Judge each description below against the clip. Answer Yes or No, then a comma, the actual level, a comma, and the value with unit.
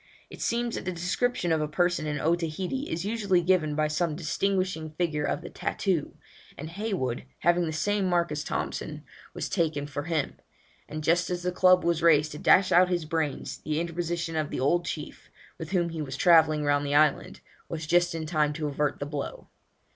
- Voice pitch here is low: No, medium, 165 Hz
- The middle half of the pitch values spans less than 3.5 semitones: Yes, average, 2.7 semitones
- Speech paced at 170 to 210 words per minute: Yes, average, 200 wpm